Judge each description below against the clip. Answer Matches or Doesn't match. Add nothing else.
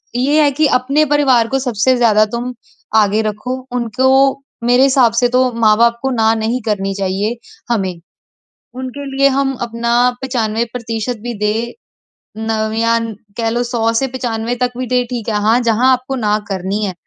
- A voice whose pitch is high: Matches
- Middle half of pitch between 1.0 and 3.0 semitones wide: Matches